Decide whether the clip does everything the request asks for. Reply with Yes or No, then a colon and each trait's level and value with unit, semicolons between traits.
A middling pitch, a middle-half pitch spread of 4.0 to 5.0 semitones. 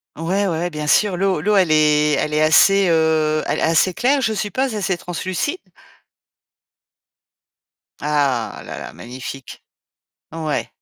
Yes: medium, 165 Hz; average, 4.4 semitones